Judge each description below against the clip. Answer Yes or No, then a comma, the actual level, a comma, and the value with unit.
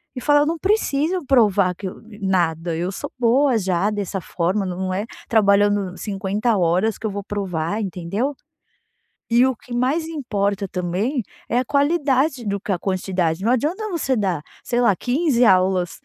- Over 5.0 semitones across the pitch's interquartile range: Yes, wide, 5.5 semitones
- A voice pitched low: No, high, 205 Hz